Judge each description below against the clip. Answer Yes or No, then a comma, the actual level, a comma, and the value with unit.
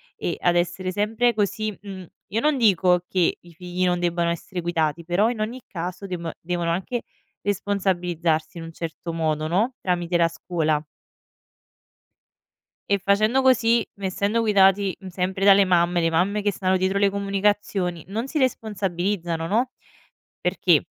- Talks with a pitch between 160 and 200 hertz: Yes, medium, 185 Hz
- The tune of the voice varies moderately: Yes, average, 3.0 semitones